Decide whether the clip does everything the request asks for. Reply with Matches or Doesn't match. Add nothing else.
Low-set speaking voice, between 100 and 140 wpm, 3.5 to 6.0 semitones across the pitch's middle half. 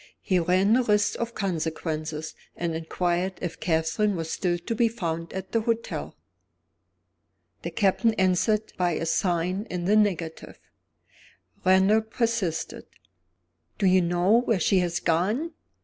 Doesn't match